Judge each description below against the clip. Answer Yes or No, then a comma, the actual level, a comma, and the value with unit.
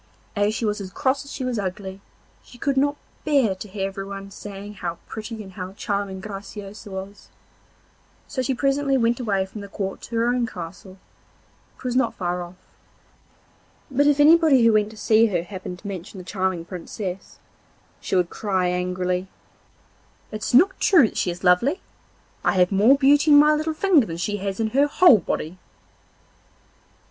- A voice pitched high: Yes, high, 205 Hz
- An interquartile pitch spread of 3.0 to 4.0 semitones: No, average, 5.3 semitones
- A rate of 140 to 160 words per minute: No, average, 180 wpm